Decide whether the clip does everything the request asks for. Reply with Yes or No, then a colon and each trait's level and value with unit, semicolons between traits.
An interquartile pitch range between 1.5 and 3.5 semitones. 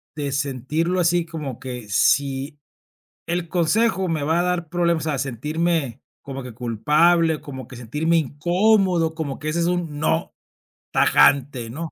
No: average, 3.9 semitones